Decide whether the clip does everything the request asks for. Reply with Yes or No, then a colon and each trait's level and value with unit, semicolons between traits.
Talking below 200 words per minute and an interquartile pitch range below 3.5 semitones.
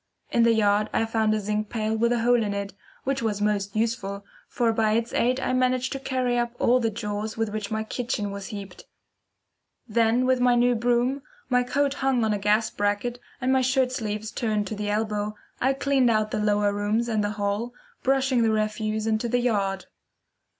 No: fast, 205 wpm; average, 2.8 semitones